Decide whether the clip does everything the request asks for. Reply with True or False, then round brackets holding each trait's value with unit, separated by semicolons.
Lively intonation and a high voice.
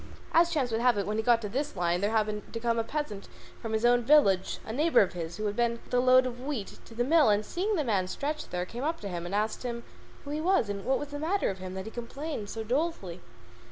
True (5.8 semitones; 235 Hz)